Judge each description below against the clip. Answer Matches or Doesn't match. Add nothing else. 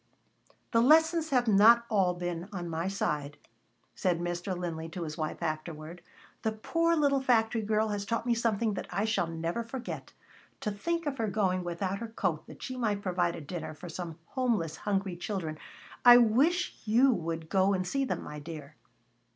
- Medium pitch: Doesn't match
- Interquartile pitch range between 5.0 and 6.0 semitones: Matches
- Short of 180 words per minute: Doesn't match